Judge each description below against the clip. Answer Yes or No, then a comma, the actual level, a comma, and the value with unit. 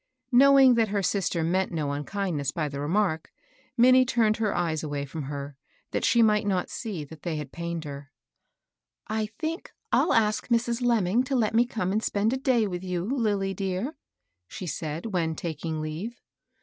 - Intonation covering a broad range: Yes, wide, 6.2 semitones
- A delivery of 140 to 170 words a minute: No, average, 185 wpm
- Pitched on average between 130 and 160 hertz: No, high, 190 Hz